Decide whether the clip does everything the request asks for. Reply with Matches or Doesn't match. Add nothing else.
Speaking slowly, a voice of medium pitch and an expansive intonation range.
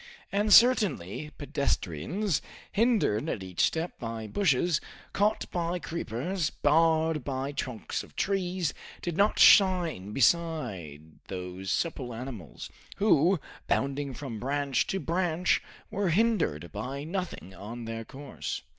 Matches